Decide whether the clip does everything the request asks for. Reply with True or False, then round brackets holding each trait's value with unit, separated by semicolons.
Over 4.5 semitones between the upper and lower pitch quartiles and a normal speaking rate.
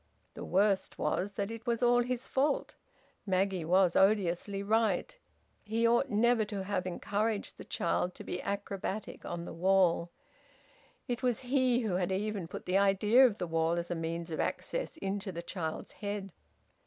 False (3.9 semitones; 170 wpm)